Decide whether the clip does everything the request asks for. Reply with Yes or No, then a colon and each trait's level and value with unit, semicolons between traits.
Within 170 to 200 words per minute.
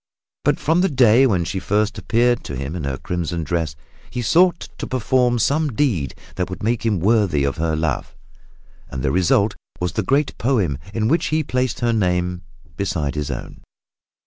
Yes: average, 185 wpm